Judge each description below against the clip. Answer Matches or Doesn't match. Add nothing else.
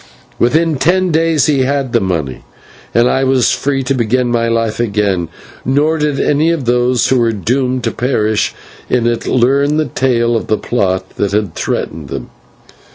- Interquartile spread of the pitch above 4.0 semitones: Doesn't match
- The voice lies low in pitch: Matches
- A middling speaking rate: Matches